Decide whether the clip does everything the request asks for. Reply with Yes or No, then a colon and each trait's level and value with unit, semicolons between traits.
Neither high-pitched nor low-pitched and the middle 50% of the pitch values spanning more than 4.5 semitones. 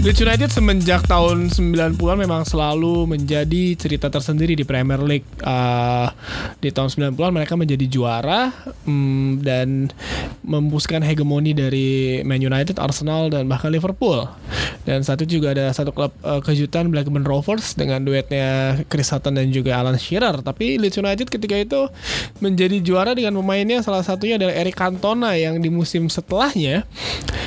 Yes: medium, 150 Hz; average, 5.1 semitones